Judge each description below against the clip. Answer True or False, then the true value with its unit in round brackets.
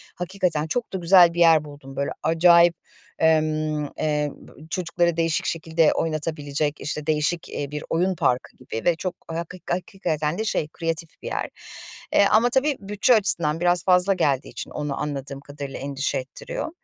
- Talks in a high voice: False (165 Hz)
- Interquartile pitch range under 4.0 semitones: True (3.0 semitones)